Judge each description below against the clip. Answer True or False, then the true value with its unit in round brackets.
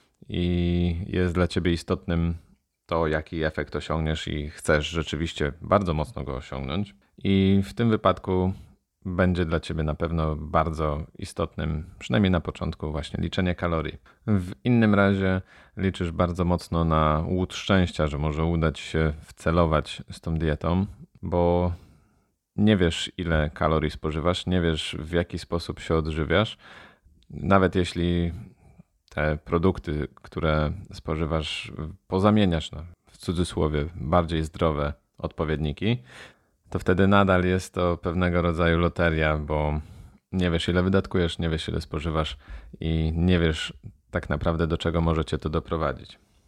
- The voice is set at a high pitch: False (85 Hz)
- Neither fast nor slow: True (135 wpm)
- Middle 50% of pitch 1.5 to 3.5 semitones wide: True (2.9 semitones)